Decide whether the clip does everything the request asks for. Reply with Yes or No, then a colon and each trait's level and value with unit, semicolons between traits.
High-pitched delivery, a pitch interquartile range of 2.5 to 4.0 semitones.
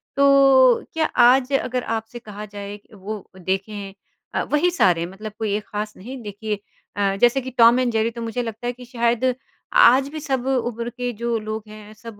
Yes: high, 230 Hz; average, 3.2 semitones